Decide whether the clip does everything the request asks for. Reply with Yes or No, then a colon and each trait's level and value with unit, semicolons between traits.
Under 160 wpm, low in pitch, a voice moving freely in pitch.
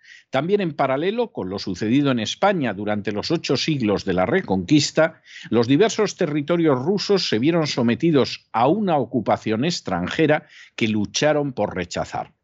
No: average, 145 wpm; medium, 145 Hz; wide, 8.4 semitones